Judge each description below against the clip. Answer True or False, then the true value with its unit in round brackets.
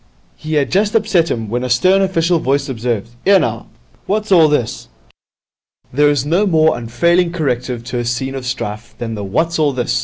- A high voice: False (145 Hz)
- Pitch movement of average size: False (6.0 semitones)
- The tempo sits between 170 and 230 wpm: True (190 wpm)